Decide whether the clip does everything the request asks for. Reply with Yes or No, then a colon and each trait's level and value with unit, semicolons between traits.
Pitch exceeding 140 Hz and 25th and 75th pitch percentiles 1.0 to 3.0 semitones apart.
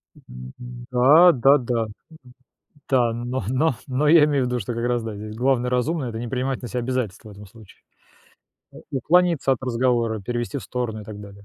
No: low, 125 Hz; narrow, 2.6 semitones